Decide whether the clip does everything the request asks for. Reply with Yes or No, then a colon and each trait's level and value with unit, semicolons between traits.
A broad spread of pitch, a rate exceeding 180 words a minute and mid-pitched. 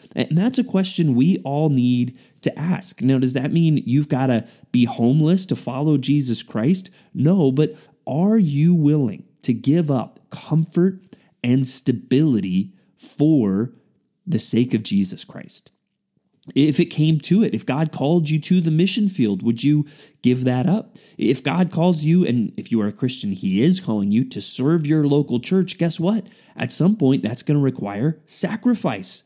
No: wide, 5.7 semitones; average, 175 wpm; medium, 155 Hz